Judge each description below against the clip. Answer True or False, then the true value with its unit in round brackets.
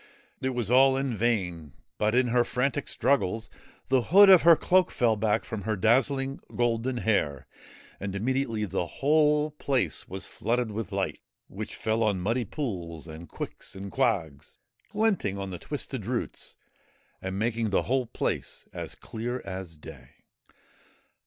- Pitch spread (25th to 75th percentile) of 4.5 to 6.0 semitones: True (5.2 semitones)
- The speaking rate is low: False (150 wpm)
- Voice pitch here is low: True (115 Hz)